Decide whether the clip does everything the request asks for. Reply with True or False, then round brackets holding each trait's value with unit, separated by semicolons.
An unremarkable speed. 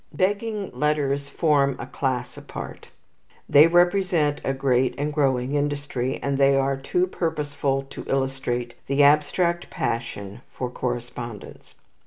False (125 wpm)